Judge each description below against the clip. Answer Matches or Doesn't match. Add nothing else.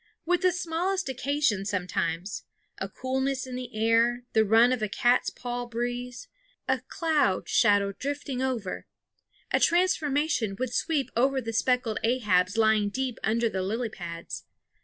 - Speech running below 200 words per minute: Matches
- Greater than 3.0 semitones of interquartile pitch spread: Matches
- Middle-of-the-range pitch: Doesn't match